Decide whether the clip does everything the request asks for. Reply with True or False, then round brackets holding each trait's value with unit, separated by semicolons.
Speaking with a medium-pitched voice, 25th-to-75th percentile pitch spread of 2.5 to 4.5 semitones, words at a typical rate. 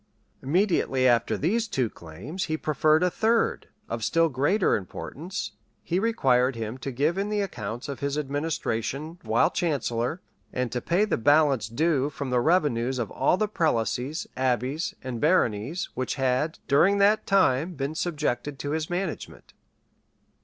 False (145 Hz; 5.6 semitones; 155 wpm)